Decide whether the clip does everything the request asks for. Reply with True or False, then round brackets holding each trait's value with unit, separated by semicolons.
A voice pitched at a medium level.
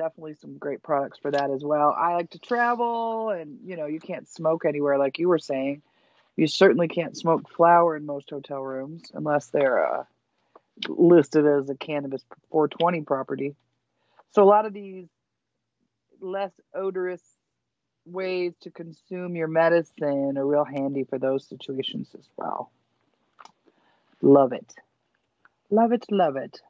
True (160 Hz)